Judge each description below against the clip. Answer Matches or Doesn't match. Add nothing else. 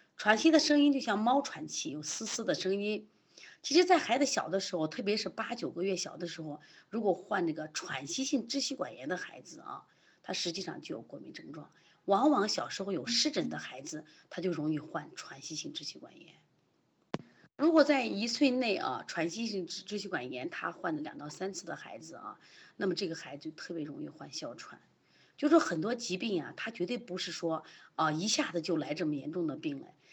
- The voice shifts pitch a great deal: Matches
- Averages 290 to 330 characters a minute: Matches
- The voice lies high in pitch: Matches